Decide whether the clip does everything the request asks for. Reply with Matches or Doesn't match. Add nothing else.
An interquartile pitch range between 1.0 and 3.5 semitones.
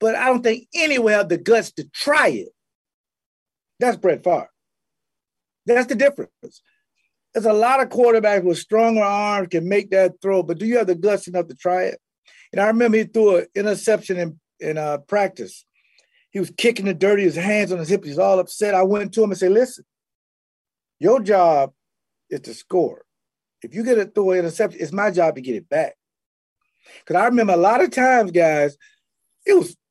Doesn't match